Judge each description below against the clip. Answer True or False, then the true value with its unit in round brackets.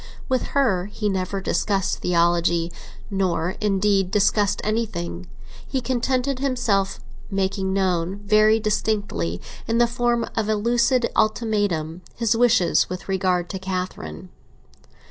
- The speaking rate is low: True (125 wpm)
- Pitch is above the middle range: True (200 Hz)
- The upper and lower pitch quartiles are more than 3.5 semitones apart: True (3.9 semitones)